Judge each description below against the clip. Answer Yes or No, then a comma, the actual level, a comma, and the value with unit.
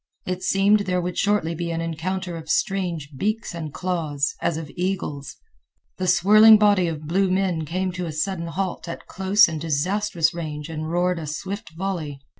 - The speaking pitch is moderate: Yes, medium, 175 Hz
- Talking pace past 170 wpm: Yes, average, 180 wpm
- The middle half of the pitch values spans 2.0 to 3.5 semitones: Yes, average, 3.1 semitones